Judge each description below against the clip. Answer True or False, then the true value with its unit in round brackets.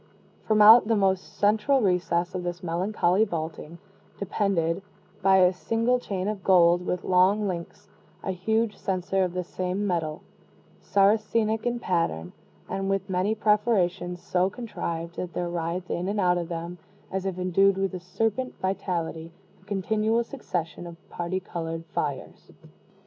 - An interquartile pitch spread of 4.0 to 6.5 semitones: False (3.0 semitones)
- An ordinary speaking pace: True (150 wpm)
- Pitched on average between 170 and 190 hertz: True (185 Hz)